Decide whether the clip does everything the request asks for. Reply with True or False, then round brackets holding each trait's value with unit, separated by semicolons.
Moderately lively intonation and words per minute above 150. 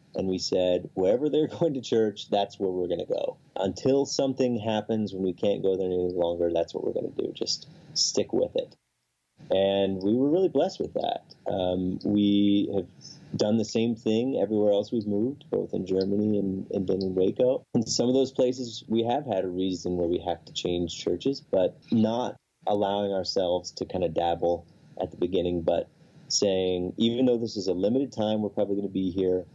True (3.9 semitones; 200 wpm)